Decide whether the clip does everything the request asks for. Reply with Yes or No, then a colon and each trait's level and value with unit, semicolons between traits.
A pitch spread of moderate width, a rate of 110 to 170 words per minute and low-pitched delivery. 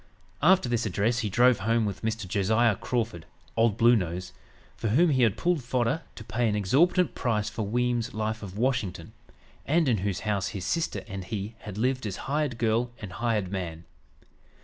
No: average, 3.3 semitones; average, 185 wpm; low, 115 Hz